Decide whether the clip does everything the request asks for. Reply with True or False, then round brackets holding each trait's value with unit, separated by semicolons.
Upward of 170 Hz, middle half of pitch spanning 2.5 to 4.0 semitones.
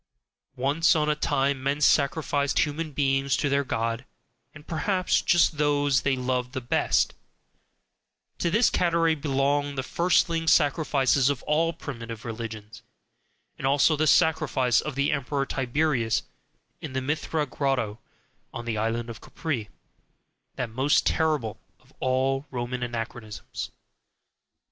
False (140 Hz; 3.4 semitones)